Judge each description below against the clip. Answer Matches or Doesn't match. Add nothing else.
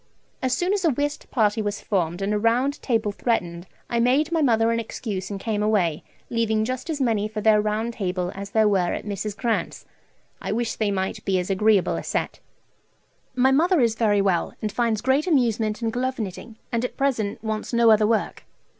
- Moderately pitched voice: Doesn't match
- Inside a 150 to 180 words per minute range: Doesn't match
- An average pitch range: Matches